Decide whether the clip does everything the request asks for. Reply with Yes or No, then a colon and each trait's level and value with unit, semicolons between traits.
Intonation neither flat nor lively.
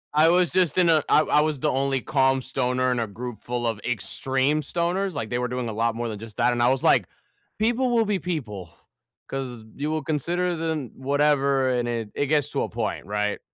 Yes: average, 4.5 semitones